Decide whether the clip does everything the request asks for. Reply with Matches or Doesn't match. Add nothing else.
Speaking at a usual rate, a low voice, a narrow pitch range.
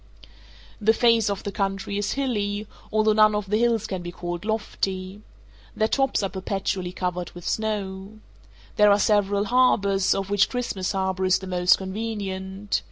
Doesn't match